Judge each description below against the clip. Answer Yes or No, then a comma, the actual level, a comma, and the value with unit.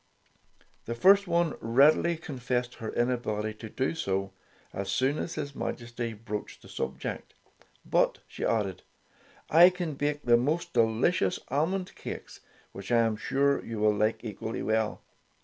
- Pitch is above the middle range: No, low, 120 Hz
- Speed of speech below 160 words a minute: Yes, average, 150 wpm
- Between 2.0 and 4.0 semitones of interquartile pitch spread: No, average, 5.2 semitones